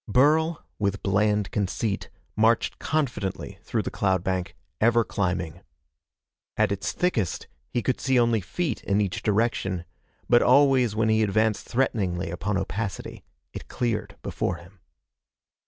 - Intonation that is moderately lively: Yes, average, 3.7 semitones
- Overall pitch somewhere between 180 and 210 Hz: No, low, 105 Hz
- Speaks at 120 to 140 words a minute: Yes, slow, 135 wpm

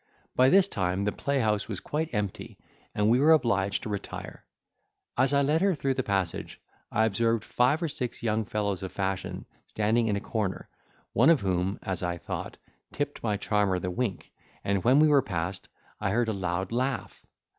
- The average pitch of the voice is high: No, low, 105 Hz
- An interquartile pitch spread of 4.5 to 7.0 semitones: Yes, average, 5.1 semitones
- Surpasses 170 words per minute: Yes, average, 190 wpm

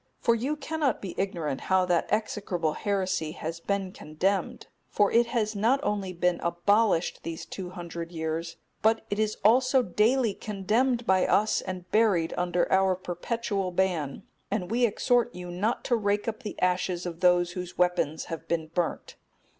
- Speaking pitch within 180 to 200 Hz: Yes, high, 190 Hz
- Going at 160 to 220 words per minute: Yes, average, 165 wpm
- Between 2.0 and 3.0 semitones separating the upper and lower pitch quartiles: No, average, 3.8 semitones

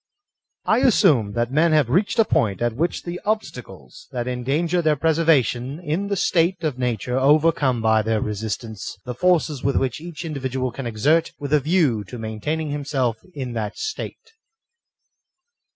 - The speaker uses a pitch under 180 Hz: Yes, medium, 140 Hz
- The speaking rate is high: No, average, 160 wpm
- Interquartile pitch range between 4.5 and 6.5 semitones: Yes, wide, 5.5 semitones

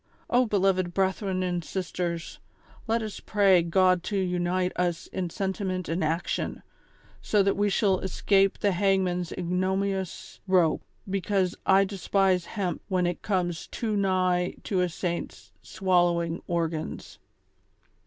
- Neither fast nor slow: No, slow, 130 wpm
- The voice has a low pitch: No, medium, 185 Hz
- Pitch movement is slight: Yes, narrow, 1.8 semitones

